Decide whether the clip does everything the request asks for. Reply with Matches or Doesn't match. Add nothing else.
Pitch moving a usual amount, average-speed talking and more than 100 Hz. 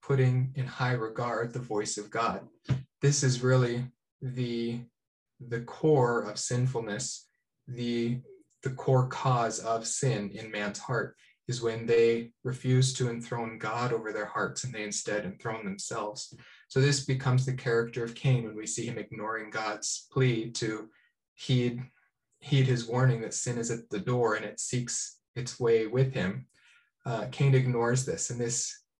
Doesn't match